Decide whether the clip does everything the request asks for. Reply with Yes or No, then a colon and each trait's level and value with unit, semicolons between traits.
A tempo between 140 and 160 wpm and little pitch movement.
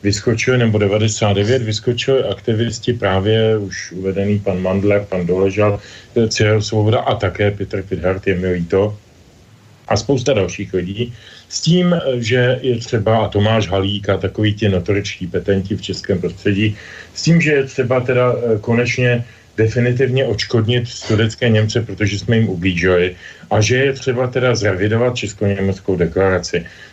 No: average, 145 wpm; average, 3.5 semitones